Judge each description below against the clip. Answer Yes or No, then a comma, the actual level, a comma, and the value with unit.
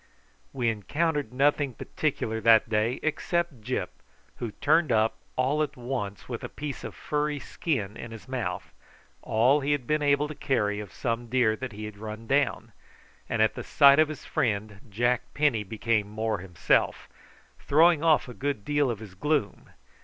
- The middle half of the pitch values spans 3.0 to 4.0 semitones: No, average, 5.0 semitones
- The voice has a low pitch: Yes, low, 125 Hz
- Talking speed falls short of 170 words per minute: No, average, 175 wpm